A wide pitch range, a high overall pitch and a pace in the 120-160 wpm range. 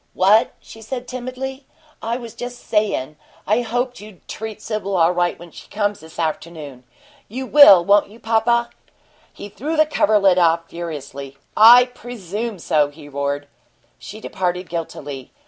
Yes: wide, 6.1 semitones; high, 205 Hz; average, 150 wpm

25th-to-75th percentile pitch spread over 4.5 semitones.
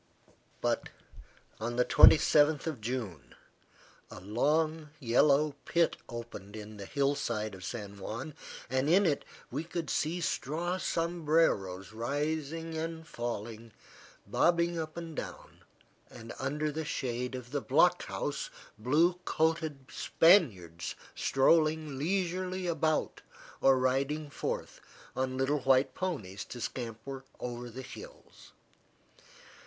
Yes: average, 5.1 semitones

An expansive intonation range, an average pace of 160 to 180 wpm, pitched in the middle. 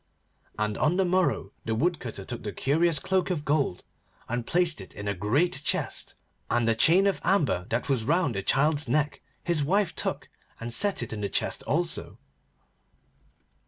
Yes: wide, 7.3 semitones; average, 175 wpm; medium, 145 Hz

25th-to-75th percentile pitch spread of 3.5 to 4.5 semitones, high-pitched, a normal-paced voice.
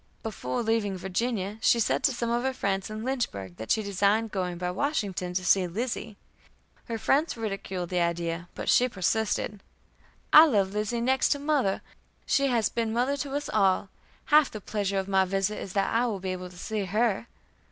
Yes: average, 4.0 semitones; high, 210 Hz; average, 195 wpm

